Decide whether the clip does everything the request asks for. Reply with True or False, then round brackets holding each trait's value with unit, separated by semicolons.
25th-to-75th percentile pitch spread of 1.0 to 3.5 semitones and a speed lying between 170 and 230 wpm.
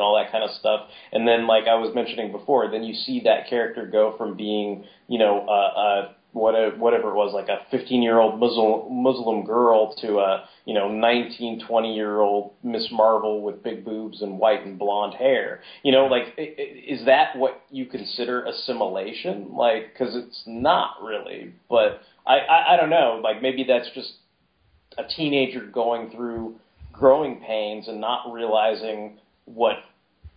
True (2.5 semitones; 180 wpm)